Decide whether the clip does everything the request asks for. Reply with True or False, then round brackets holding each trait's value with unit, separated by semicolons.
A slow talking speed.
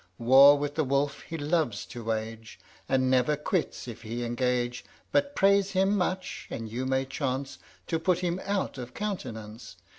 False (170 wpm)